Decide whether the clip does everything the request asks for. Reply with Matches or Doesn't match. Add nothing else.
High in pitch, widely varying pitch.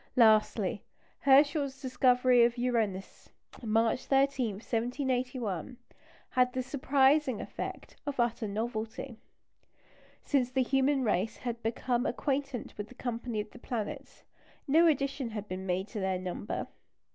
Doesn't match